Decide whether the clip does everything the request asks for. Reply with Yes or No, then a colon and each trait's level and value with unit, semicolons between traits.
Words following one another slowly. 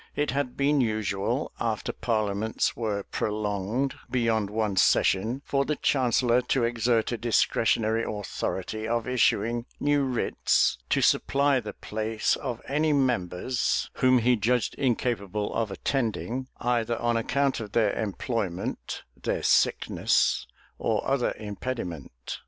Yes: slow, 125 wpm